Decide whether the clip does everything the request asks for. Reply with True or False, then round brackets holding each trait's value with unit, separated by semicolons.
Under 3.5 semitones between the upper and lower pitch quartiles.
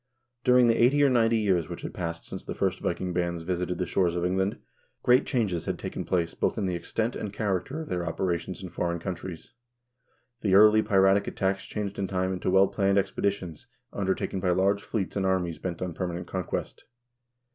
True (2.5 semitones)